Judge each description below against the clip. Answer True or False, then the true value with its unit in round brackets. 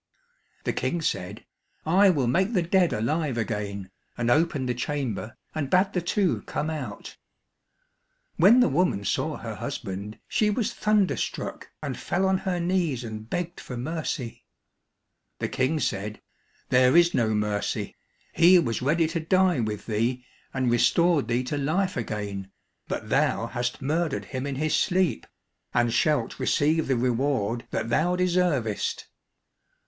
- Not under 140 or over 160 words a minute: True (150 wpm)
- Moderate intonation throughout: False (6.7 semitones)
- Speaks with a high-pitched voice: False (140 Hz)